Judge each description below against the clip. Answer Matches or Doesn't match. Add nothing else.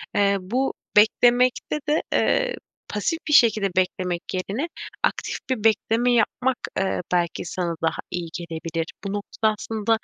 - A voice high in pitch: Matches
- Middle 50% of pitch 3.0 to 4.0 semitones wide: Doesn't match